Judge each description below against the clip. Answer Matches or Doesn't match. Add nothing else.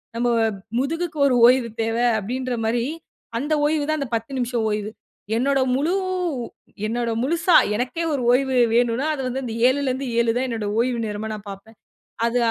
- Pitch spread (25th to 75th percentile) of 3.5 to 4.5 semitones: Doesn't match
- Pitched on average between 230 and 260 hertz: Matches